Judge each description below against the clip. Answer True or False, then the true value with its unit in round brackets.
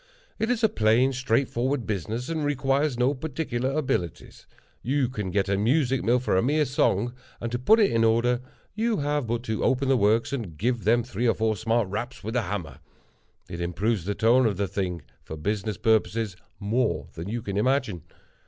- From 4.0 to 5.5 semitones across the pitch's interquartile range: True (4.3 semitones)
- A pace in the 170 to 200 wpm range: True (195 wpm)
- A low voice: True (120 Hz)